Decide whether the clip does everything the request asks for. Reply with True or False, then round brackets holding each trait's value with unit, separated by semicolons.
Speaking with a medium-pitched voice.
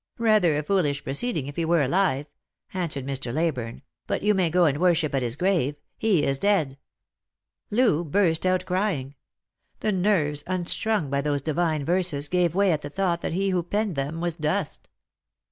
True (170 Hz)